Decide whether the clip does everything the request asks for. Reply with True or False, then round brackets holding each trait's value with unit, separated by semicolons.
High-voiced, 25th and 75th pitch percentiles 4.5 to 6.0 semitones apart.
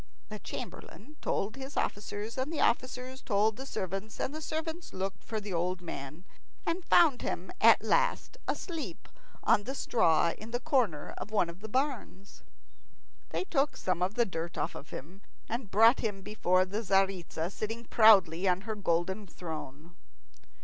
True (210 Hz; 5.6 semitones)